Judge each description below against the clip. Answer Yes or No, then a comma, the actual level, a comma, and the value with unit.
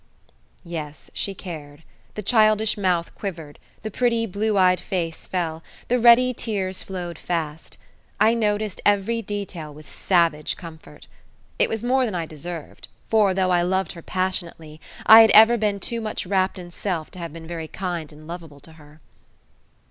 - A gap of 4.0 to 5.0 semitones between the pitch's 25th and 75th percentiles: Yes, average, 4.4 semitones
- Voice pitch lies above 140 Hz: Yes, medium, 185 Hz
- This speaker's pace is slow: No, average, 165 wpm